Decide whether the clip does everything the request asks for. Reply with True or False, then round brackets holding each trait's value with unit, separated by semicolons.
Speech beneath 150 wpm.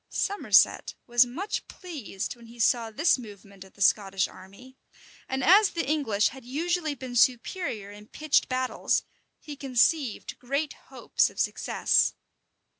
True (140 wpm)